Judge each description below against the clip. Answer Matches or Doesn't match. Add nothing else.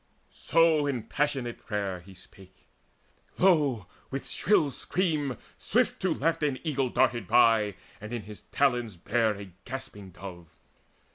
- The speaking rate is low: Matches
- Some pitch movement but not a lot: Doesn't match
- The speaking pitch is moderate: Doesn't match